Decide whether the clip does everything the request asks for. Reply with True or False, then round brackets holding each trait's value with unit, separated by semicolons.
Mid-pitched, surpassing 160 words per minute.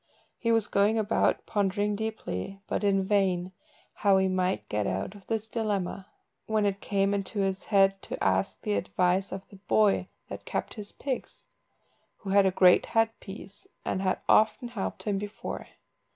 False (195 Hz; 170 wpm)